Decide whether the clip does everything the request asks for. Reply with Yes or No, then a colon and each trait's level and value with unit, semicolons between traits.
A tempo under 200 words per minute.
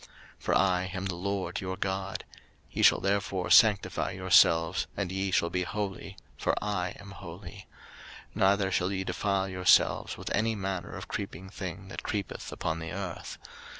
Yes: average, 165 wpm